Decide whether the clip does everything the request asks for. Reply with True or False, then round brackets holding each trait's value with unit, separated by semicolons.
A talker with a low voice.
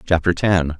True (85 Hz)